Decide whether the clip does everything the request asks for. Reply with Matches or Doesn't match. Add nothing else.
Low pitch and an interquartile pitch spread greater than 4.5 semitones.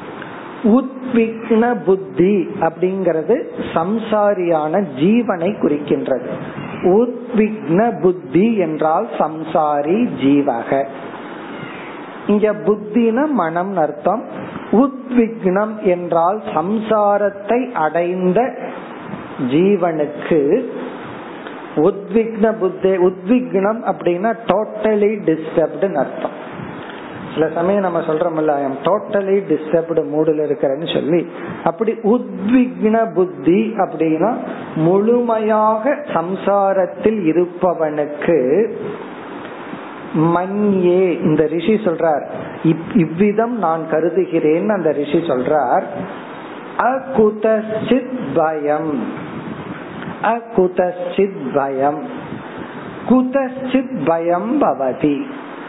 Doesn't match